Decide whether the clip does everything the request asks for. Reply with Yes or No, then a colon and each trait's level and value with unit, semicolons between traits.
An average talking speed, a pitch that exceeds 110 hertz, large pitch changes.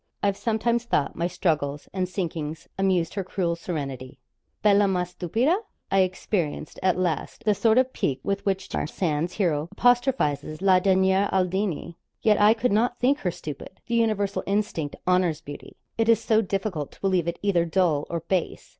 No: average, 170 wpm; medium, 185 Hz; average, 3.7 semitones